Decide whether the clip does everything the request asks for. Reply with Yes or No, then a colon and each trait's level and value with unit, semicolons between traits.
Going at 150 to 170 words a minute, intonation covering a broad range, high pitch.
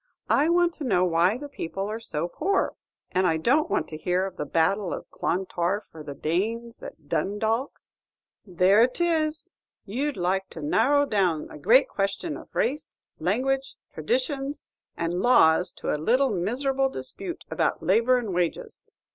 Yes: average, 165 wpm; wide, 7.4 semitones; high, 210 Hz